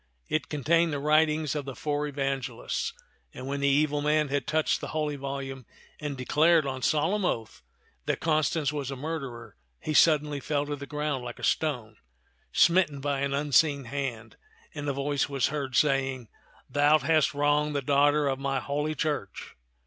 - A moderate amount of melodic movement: No, narrow, 1.8 semitones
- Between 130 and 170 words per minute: No, average, 180 wpm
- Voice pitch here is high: No, medium, 145 Hz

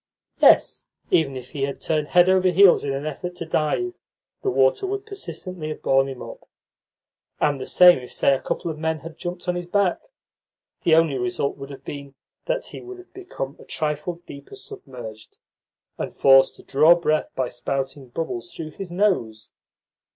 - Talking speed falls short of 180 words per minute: No, average, 185 wpm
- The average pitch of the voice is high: No, medium, 155 Hz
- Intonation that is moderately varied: Yes, average, 4.7 semitones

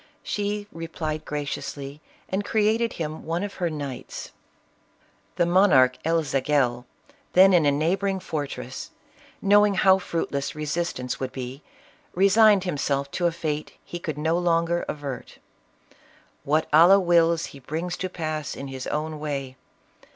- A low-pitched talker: No, medium, 160 Hz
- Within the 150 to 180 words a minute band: No, average, 140 wpm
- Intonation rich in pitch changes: No, average, 4.0 semitones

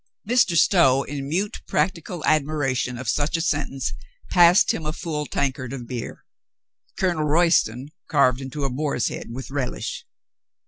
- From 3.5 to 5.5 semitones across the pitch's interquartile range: Yes, average, 4.0 semitones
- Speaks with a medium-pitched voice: Yes, medium, 145 Hz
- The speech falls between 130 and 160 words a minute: Yes, average, 145 wpm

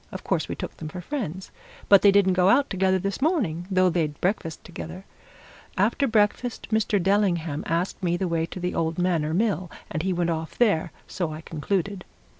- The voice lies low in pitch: No, medium, 185 Hz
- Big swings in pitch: No, average, 3.3 semitones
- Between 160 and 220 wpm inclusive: Yes, average, 200 wpm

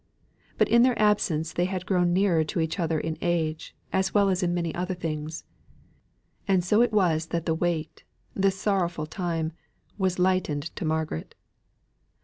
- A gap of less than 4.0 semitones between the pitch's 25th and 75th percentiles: Yes, average, 2.9 semitones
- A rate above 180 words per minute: No, average, 165 wpm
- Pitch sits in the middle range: Yes, medium, 175 Hz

